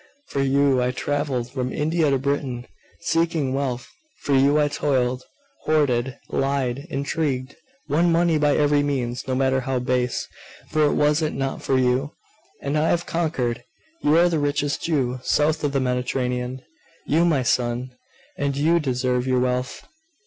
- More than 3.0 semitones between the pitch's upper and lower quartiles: No, average, 2.7 semitones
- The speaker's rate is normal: Yes, average, 155 wpm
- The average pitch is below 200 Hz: Yes, low, 135 Hz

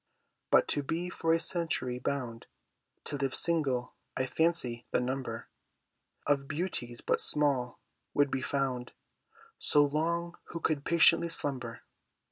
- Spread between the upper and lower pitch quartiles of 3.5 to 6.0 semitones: Yes, average, 4.5 semitones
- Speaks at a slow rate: Yes, slow, 130 wpm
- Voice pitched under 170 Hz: Yes, medium, 140 Hz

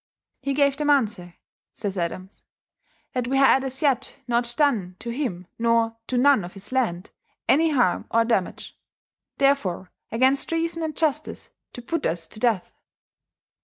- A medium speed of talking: Yes, average, 155 wpm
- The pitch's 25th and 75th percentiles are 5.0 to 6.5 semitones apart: Yes, wide, 5.4 semitones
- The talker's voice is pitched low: No, high, 245 Hz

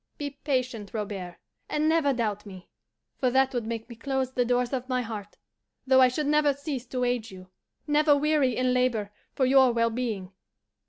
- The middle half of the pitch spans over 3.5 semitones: No, average, 3.2 semitones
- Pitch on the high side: Yes, very high, 250 Hz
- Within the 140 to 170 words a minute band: No, average, 190 wpm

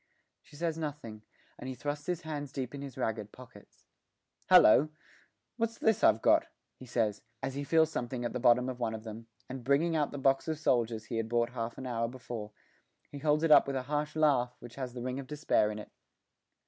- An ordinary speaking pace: No, fast, 220 wpm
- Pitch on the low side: Yes, low, 130 Hz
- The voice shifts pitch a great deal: No, average, 4.0 semitones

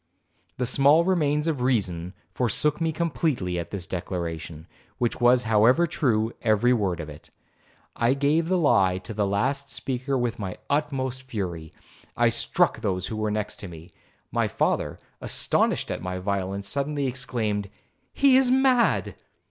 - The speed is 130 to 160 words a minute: Yes, average, 150 wpm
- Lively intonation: Yes, wide, 6.7 semitones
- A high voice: No, low, 120 Hz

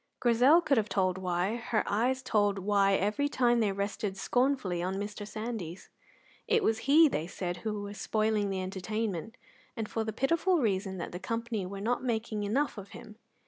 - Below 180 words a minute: No, average, 185 wpm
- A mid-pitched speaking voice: No, high, 215 Hz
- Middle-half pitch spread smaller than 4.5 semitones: Yes, average, 3.6 semitones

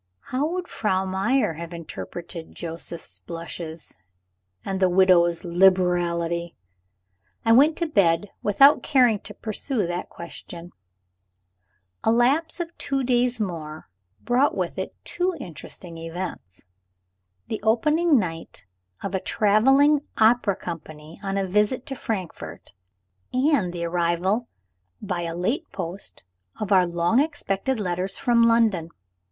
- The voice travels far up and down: Yes, wide, 6.2 semitones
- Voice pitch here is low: No, high, 195 Hz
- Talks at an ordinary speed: No, slow, 125 wpm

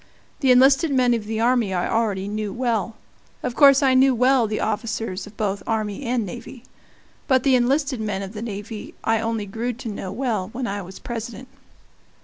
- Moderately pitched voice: No, high, 230 Hz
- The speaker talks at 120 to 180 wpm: No, average, 190 wpm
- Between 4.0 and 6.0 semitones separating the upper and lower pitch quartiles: No, average, 3.5 semitones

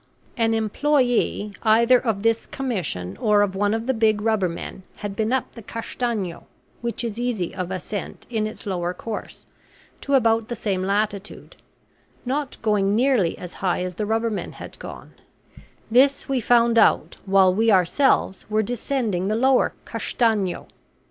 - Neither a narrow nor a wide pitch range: Yes, average, 3.3 semitones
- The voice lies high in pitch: Yes, high, 220 Hz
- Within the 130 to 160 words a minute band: Yes, average, 155 wpm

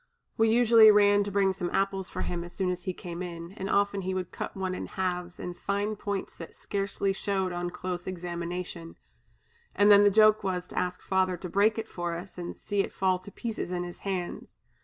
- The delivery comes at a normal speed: No, fast, 220 wpm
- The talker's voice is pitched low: No, high, 190 Hz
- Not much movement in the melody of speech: Yes, narrow, 2.2 semitones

